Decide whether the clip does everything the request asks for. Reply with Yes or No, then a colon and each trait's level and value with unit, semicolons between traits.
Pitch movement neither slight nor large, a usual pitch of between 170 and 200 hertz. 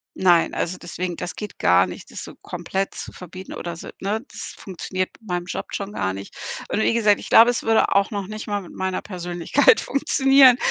Yes: average, 3.5 semitones; high, 190 Hz